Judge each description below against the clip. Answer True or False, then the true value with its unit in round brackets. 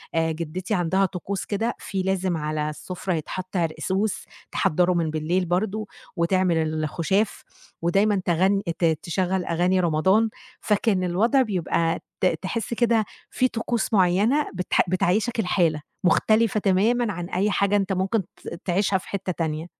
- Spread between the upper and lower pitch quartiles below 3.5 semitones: True (3.1 semitones)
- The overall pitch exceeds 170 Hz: True (185 Hz)